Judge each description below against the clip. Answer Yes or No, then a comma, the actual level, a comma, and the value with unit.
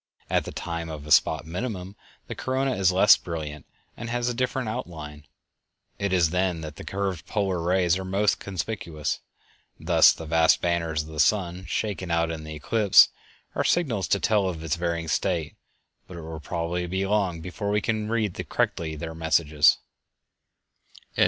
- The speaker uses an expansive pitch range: No, average, 3.7 semitones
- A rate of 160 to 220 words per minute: Yes, average, 175 wpm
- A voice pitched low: Yes, very low, 90 Hz